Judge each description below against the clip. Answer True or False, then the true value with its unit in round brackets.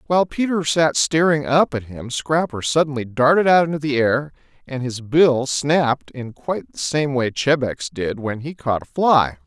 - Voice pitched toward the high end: False (140 Hz)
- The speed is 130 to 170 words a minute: False (190 wpm)